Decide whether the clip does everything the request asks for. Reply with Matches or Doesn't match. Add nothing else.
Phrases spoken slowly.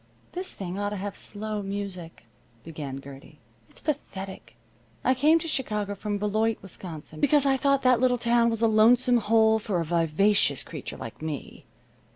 Doesn't match